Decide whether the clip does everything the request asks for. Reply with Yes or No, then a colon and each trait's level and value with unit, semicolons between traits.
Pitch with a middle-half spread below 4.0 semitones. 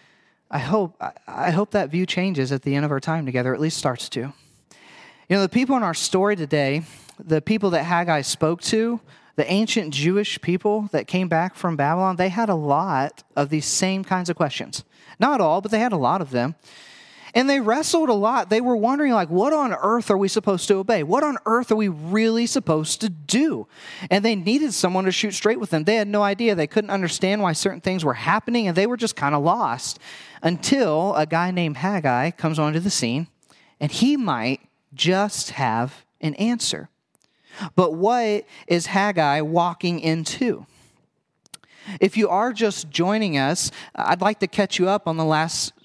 No: wide, 5.4 semitones